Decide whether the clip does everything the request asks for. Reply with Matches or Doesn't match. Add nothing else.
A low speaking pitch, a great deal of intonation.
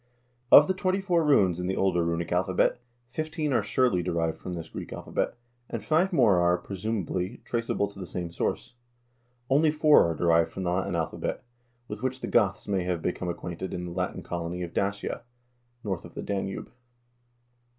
Matches